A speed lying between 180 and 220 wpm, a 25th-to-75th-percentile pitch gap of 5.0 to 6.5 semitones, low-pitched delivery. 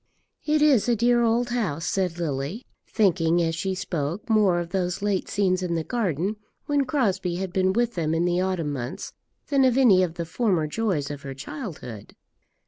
No: average, 190 wpm; wide, 5.5 semitones; medium, 185 Hz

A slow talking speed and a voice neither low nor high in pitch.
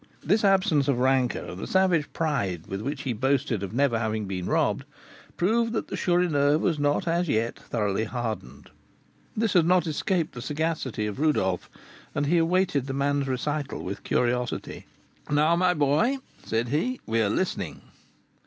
No: average, 160 wpm; medium, 145 Hz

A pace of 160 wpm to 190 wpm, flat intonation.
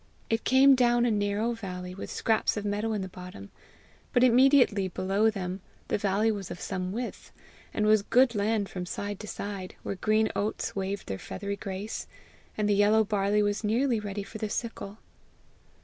Yes: average, 180 wpm; narrow, 2.2 semitones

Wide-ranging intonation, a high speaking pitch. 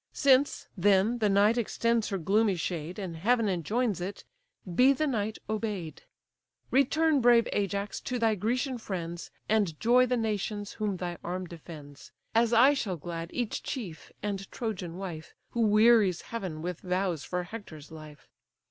No: average, 4.7 semitones; high, 205 Hz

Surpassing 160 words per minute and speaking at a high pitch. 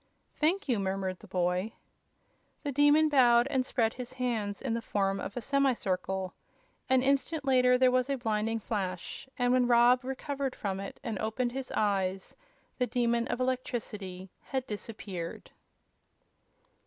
No: average, 155 wpm; high, 240 Hz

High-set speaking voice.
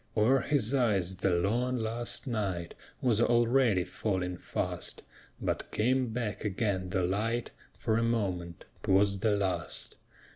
No: low, 105 Hz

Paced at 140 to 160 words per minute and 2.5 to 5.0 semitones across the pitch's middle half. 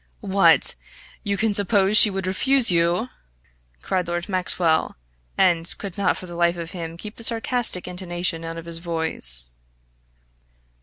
Yes: average, 150 wpm; average, 3.0 semitones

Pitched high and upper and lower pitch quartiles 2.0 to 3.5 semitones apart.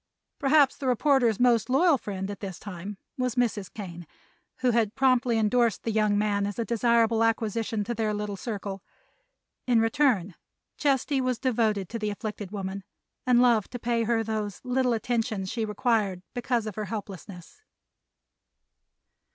Yes: high, 225 Hz; average, 3.2 semitones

